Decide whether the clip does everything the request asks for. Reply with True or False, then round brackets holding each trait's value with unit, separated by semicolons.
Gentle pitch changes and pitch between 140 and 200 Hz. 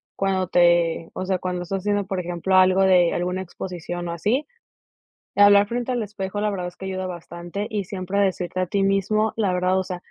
True (2.1 semitones; 185 Hz)